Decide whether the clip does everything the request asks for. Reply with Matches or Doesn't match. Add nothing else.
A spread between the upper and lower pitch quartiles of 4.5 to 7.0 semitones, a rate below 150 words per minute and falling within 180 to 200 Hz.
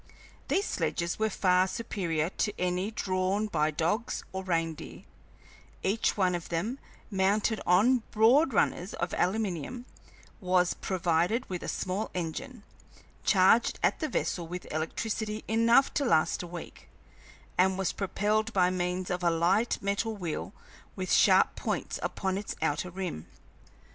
Doesn't match